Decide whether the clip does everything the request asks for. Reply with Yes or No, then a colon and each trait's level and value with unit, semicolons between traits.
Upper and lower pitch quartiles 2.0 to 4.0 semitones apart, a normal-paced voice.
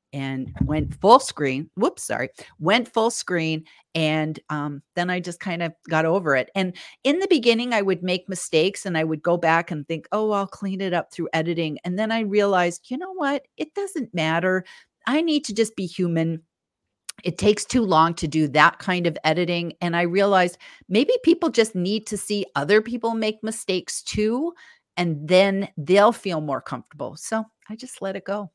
No: average, 4.8 semitones; average, 195 wpm